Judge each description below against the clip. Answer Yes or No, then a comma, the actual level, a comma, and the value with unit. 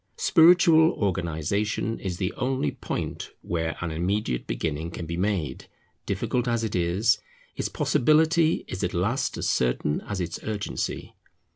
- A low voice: Yes, very low, 95 Hz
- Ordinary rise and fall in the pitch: No, wide, 5.9 semitones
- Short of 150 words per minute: Yes, average, 140 wpm